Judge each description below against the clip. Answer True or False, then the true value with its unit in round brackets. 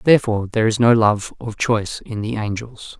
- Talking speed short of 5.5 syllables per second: False (5.6 syllables/s)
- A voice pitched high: False (110 Hz)